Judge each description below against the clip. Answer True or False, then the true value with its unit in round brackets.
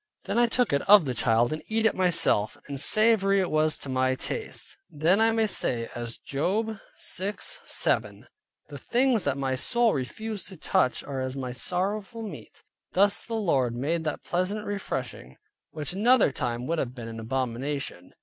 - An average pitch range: False (8.2 semitones)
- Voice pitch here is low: False (160 Hz)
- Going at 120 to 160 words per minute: False (175 wpm)